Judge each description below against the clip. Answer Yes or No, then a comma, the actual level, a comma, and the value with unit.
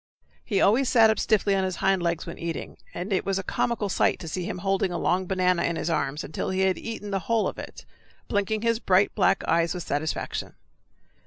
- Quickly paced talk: Yes, fast, 225 wpm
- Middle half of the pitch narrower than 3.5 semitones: Yes, average, 2.8 semitones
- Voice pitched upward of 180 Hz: Yes, high, 190 Hz